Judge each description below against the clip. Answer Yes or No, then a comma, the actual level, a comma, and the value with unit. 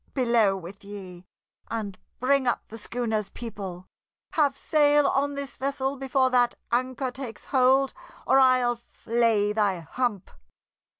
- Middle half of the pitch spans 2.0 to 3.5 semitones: No, average, 4.3 semitones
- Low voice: No, high, 245 Hz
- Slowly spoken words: Yes, slow, 130 wpm